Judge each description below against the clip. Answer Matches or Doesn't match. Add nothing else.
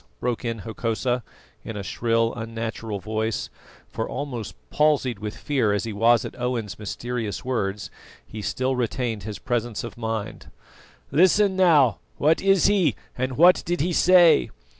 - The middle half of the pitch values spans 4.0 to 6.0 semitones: Matches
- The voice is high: Doesn't match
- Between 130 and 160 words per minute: Matches